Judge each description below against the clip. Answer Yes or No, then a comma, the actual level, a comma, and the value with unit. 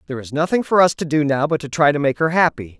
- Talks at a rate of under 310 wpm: No, fast, 320 wpm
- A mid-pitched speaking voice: Yes, medium, 150 Hz